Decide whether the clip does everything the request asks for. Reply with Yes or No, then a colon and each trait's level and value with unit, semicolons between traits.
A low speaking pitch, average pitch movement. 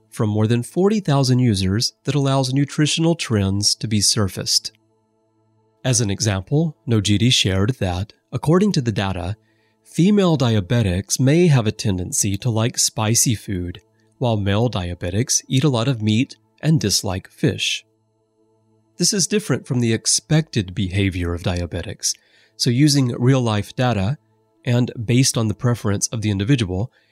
Yes: low, 110 Hz; average, 4.1 semitones